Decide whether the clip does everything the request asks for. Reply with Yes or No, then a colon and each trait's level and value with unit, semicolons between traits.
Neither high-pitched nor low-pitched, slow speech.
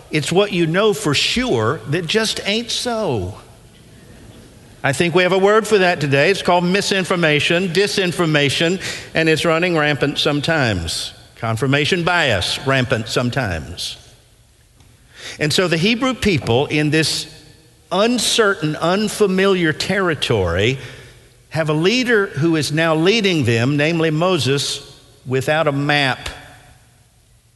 Yes: medium, 155 Hz; slow, 120 wpm